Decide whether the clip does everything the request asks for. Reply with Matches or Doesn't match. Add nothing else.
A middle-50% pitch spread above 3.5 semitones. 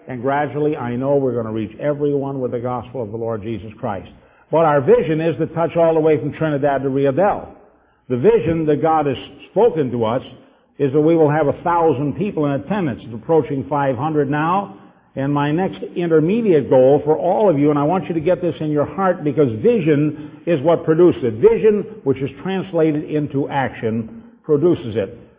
Doesn't match